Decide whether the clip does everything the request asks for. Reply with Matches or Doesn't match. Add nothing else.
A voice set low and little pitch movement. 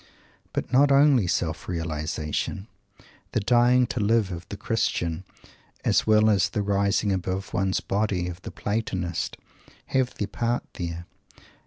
Doesn't match